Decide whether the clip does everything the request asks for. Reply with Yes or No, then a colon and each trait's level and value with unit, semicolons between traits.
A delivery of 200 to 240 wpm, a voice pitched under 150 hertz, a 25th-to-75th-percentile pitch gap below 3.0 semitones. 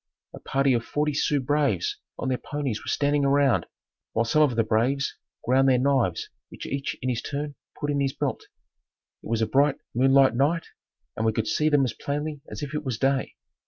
Yes: fast, 205 wpm; medium, 140 Hz; narrow, 2.5 semitones